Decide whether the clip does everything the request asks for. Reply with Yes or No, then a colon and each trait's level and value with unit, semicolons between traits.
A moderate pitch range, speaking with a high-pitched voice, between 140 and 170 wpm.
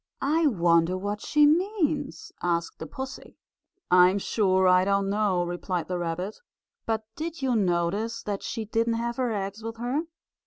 Yes: average, 4.6 semitones; high, 205 Hz; average, 160 wpm